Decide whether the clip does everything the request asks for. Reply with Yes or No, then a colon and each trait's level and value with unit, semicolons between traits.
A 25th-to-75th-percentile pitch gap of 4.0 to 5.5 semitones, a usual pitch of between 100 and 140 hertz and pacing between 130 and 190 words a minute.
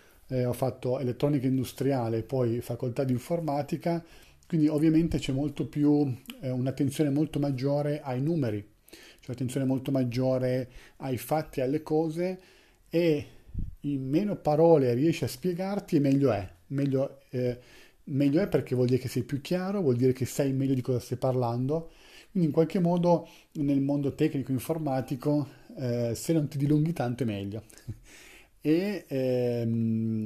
No: average, 3.5 semitones; low, 135 Hz; average, 150 wpm